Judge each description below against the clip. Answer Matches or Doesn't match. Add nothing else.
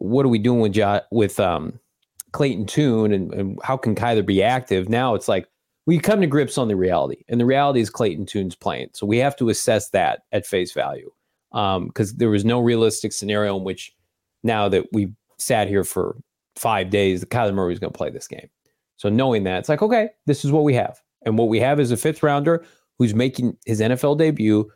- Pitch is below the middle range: Matches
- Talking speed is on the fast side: Matches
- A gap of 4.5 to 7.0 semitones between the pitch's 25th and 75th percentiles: Matches